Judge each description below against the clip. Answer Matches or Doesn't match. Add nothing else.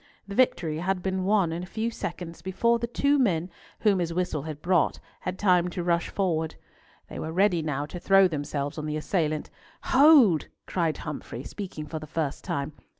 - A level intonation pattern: Doesn't match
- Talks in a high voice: Doesn't match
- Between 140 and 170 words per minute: Doesn't match